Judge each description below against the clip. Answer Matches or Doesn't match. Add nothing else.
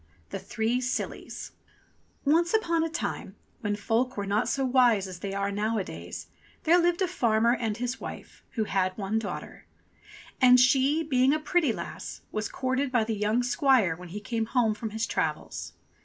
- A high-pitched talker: Matches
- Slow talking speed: Doesn't match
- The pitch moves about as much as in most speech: Matches